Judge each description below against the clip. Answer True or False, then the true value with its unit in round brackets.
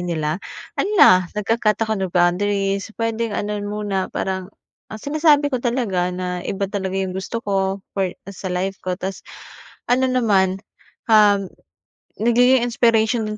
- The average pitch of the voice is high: True (200 Hz)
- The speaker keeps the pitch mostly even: False (3.4 semitones)